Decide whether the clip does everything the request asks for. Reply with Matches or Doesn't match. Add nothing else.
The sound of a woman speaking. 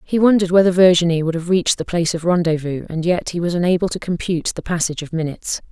Matches